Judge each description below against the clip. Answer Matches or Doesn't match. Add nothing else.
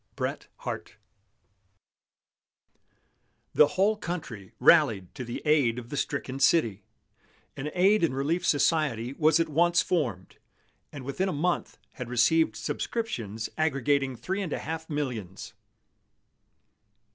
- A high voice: Doesn't match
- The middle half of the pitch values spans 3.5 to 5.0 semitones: Doesn't match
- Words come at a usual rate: Doesn't match